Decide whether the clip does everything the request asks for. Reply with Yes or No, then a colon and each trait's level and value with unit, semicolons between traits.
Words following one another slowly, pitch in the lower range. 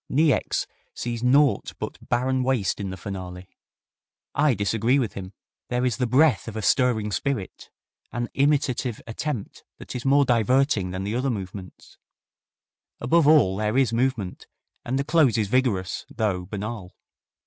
No: average, 150 wpm; low, 120 Hz